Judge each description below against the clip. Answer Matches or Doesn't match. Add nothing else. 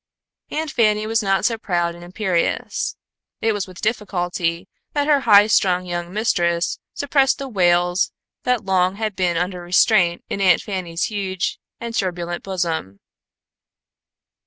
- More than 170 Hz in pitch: Matches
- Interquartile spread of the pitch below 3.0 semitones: Doesn't match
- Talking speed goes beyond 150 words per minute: Doesn't match